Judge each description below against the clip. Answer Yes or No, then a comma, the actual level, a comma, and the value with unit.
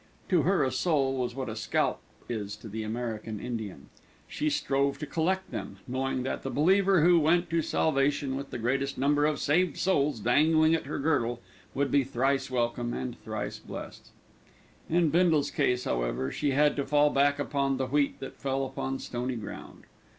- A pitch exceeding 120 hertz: Yes, low, 135 Hz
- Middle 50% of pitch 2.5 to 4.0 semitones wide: Yes, average, 3.7 semitones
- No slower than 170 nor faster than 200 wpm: Yes, average, 180 wpm